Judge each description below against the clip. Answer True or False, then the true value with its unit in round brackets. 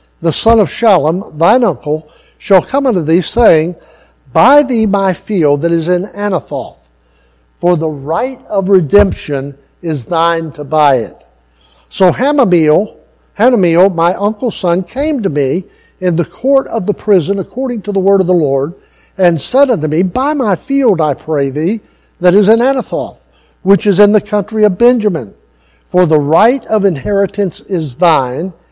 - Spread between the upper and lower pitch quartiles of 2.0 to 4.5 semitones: False (5.1 semitones)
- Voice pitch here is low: False (180 Hz)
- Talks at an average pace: True (165 wpm)